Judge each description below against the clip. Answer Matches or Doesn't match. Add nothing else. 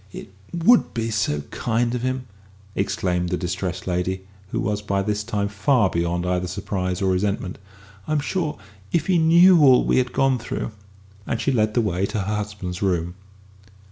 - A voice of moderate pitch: Doesn't match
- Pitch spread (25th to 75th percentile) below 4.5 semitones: Doesn't match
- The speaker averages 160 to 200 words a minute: Matches